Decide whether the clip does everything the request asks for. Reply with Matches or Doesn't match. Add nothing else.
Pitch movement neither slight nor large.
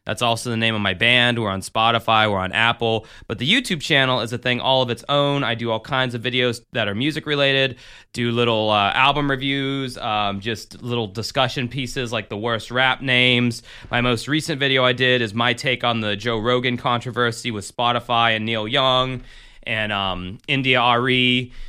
Doesn't match